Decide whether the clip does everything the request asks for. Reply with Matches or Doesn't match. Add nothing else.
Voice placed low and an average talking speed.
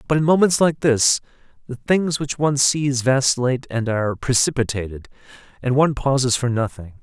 Matches